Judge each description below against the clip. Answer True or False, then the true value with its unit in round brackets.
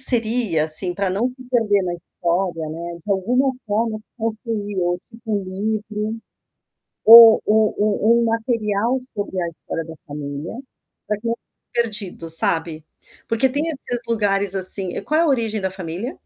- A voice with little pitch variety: False (4.2 semitones)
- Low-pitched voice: False (210 Hz)